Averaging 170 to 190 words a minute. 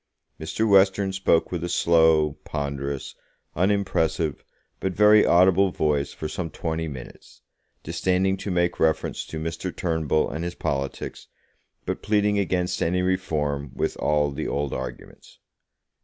No: slow, 135 wpm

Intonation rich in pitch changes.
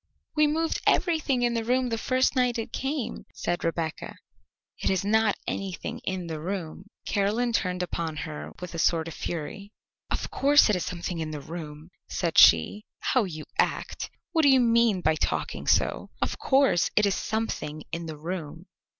Yes: wide, 6.5 semitones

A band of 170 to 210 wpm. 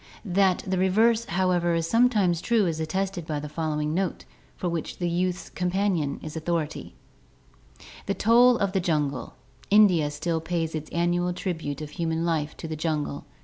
Yes: average, 175 wpm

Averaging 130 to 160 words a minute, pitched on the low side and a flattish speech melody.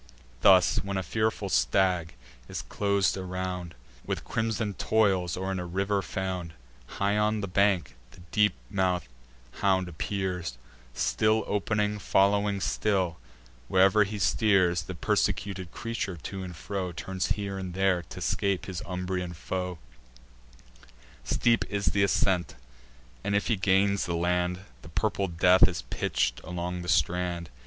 Yes: average, 140 wpm; very low, 95 Hz; narrow, 2.1 semitones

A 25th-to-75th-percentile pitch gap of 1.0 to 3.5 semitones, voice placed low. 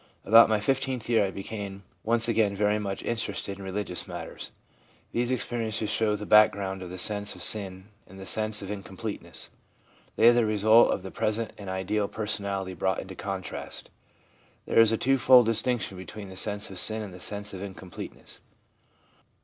Yes: narrow, 2.5 semitones; low, 105 Hz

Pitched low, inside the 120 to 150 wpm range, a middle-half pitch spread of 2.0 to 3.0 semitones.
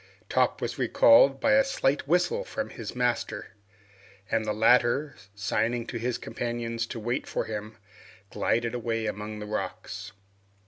Yes: low, 115 Hz; average, 145 wpm; narrow, 2.5 semitones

